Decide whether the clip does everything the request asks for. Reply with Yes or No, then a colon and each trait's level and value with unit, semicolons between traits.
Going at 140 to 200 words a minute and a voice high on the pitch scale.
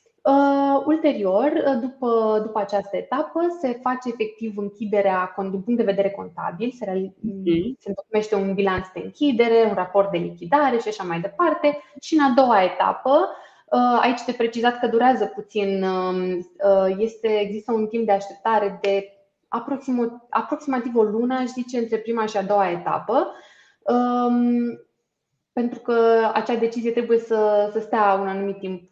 Yes: average, 155 wpm; high, 225 Hz